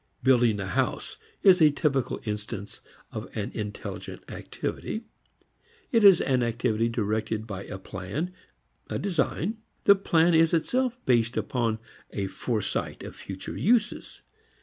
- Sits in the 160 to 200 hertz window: No, low, 120 Hz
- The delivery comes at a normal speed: No, slow, 130 wpm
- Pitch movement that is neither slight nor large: No, wide, 8.1 semitones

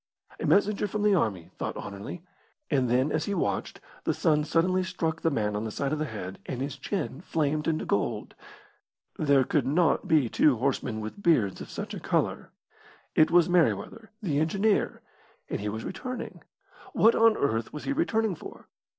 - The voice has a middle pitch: Yes, medium, 155 Hz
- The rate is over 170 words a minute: Yes, average, 185 wpm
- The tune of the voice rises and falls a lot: Yes, wide, 6.8 semitones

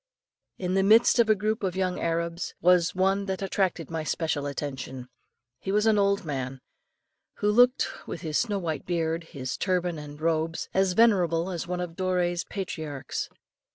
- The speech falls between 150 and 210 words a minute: Yes, average, 170 wpm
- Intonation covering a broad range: No, average, 3.2 semitones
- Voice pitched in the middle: Yes, medium, 180 Hz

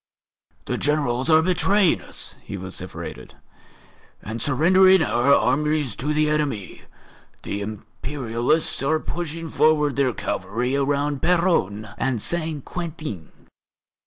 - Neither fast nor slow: No, slow, 110 wpm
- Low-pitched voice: No, medium, 145 Hz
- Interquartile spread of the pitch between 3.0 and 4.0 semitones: No, average, 4.6 semitones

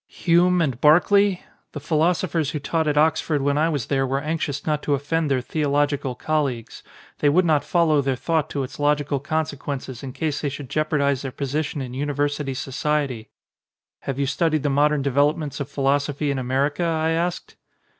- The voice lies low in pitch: No, medium, 145 Hz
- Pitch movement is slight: Yes, narrow, 2.2 semitones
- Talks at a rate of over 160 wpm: Yes, average, 180 wpm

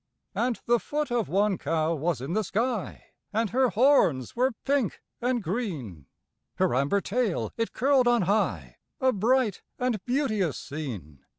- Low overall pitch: No, high, 215 Hz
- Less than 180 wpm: Yes, average, 155 wpm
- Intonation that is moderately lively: No, wide, 7.6 semitones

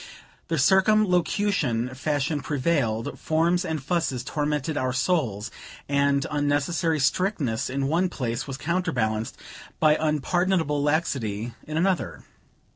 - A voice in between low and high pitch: Yes, medium, 150 Hz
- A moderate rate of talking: No, slow, 110 wpm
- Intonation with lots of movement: No, average, 4.5 semitones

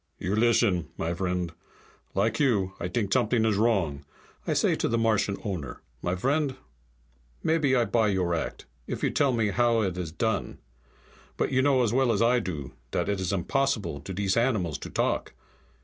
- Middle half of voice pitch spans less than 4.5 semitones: No, average, 4.8 semitones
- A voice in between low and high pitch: No, low, 105 Hz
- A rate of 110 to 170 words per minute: No, average, 180 wpm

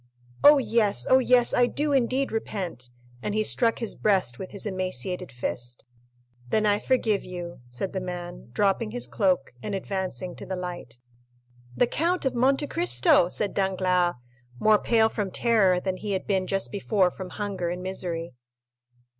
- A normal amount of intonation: Yes, average, 4.1 semitones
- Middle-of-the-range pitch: No, high, 195 Hz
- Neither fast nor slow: Yes, average, 165 wpm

